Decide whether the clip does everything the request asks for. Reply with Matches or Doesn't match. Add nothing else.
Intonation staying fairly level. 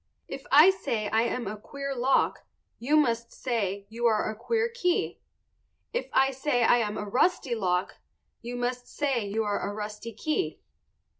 Doesn't match